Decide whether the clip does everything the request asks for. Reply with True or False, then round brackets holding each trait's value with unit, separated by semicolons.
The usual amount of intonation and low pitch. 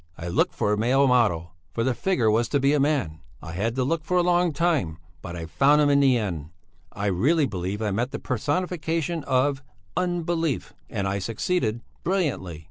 False (7.5 semitones; 130 Hz)